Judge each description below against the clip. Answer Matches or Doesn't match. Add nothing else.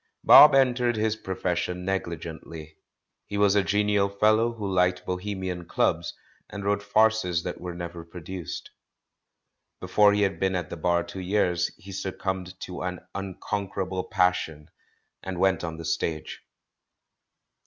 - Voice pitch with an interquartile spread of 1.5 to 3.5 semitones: Matches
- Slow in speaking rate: Doesn't match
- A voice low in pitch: Matches